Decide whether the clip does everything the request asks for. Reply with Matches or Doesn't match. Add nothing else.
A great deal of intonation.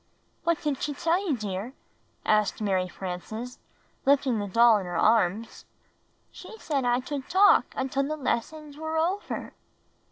Matches